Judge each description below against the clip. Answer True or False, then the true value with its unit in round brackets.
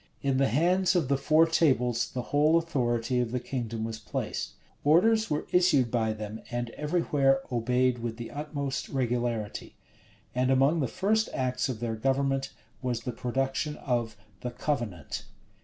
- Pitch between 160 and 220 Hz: False (130 Hz)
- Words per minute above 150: True (160 wpm)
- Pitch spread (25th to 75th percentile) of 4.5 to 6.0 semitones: False (3.8 semitones)